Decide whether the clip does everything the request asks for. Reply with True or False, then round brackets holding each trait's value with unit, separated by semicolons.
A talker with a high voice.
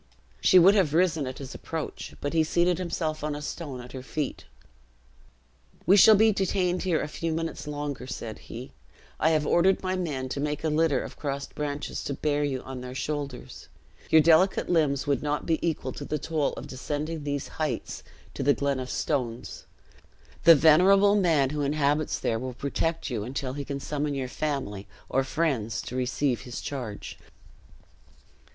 False (145 Hz)